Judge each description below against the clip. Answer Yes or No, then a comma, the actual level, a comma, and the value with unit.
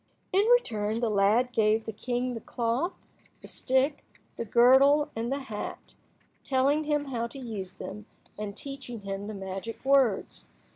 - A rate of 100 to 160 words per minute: Yes, average, 155 wpm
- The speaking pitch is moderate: No, high, 235 Hz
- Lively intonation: No, average, 4.3 semitones